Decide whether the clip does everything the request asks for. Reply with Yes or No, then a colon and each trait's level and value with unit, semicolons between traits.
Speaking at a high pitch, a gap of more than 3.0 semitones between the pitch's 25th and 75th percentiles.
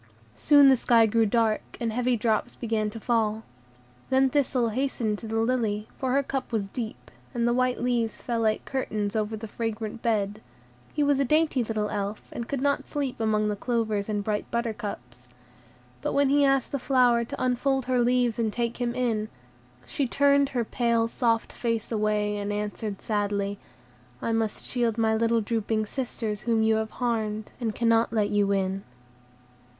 No: high, 230 Hz; average, 2.7 semitones